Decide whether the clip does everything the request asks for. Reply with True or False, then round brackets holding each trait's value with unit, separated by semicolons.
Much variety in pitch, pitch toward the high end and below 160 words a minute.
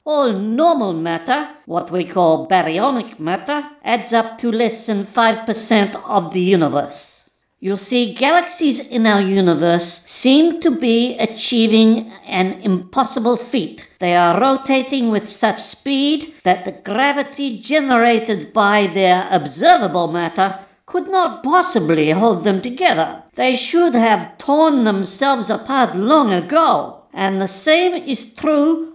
True (6.1 semitones; 230 Hz; 135 wpm)